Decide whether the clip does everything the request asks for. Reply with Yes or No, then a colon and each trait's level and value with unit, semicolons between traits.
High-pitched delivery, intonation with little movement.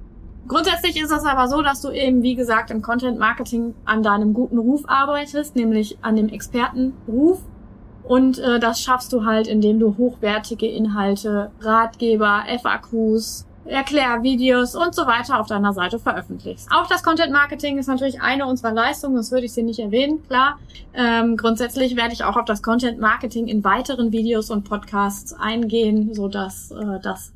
No: high, 235 Hz; average, 3.1 semitones